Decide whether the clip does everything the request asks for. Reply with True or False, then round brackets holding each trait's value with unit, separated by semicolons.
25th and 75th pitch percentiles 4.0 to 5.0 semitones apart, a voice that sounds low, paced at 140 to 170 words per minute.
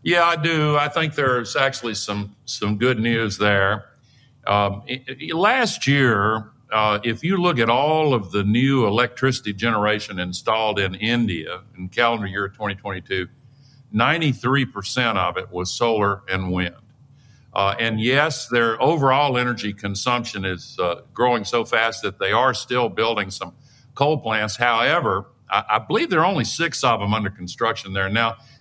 True (4.4 semitones; 115 Hz; 155 wpm)